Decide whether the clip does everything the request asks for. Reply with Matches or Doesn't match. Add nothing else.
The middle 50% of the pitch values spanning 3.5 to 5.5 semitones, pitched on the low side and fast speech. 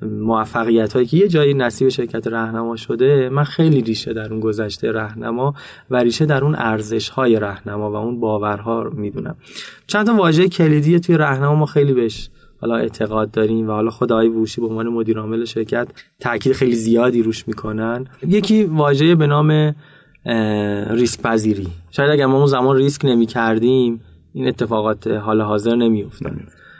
Matches